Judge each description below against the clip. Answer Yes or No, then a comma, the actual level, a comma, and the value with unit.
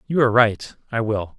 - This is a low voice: Yes, low, 115 Hz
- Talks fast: No, average, 175 wpm